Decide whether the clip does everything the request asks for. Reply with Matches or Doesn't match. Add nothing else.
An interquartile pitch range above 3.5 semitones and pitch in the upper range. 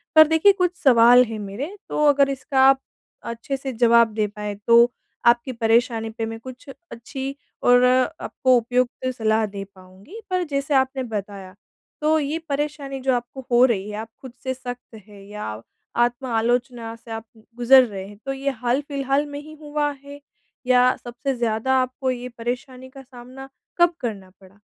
Doesn't match